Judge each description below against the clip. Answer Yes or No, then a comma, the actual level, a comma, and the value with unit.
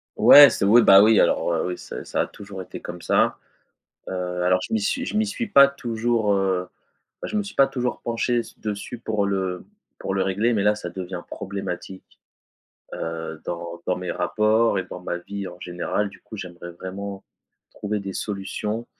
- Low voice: Yes, low, 100 Hz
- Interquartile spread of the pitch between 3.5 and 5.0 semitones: Yes, average, 3.9 semitones